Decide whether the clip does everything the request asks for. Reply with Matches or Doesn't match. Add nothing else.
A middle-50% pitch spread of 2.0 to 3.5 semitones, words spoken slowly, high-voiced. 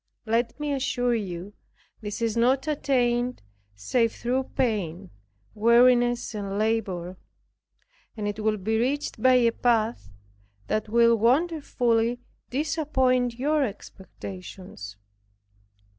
Matches